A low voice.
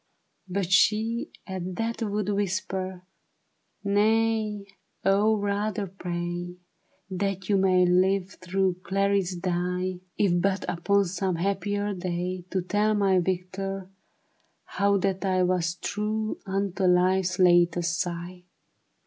No: high, 190 Hz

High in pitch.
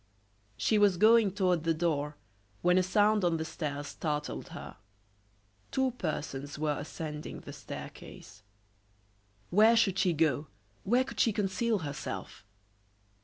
No: medium, 175 Hz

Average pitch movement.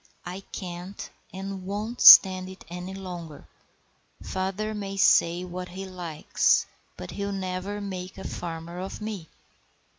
No: narrow, 1.7 semitones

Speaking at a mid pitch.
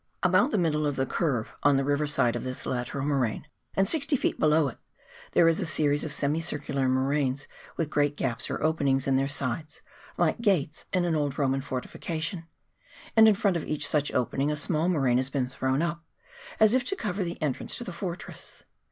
Yes: medium, 150 Hz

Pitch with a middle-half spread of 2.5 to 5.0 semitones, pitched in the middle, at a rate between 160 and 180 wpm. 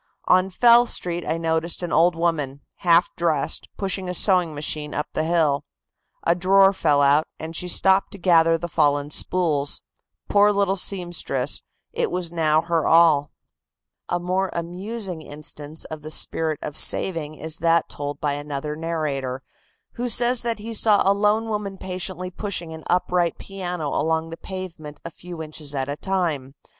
Yes: average, 3.5 semitones; medium, 170 Hz; average, 165 wpm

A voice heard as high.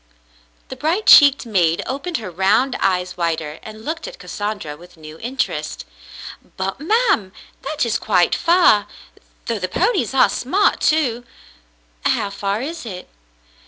Yes: high, 220 Hz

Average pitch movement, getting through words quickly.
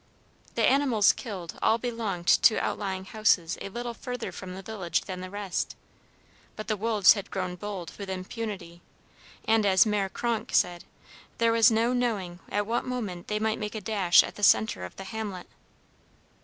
No: average, 3.4 semitones; average, 175 wpm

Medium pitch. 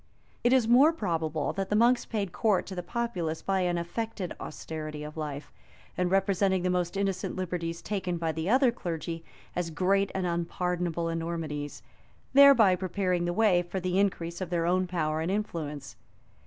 Yes: medium, 180 Hz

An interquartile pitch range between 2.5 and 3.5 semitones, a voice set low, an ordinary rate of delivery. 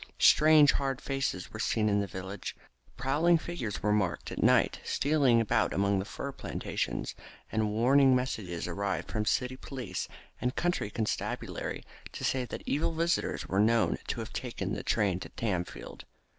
No: average, 5.3 semitones; low, 115 Hz; average, 160 wpm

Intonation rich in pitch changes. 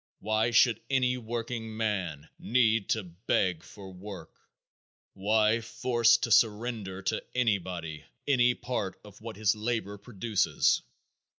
No: average, 3.4 semitones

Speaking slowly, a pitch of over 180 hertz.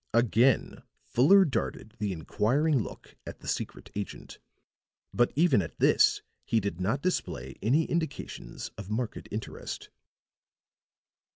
No: slow, 120 wpm; low, 115 Hz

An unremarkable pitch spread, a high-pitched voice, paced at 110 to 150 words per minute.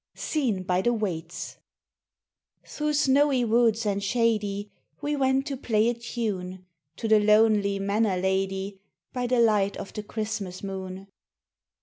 Yes: average, 3.6 semitones; high, 210 Hz; slow, 135 wpm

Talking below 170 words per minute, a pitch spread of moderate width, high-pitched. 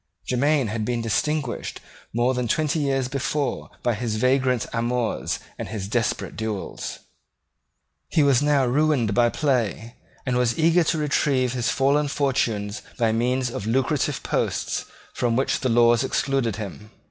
No: average, 145 wpm; average, 3.1 semitones; low, 125 Hz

